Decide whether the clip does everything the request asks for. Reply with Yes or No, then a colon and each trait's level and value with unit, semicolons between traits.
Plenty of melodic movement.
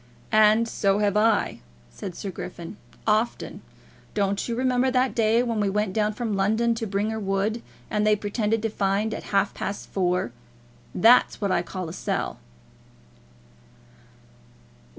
No: narrow, 2.4 semitones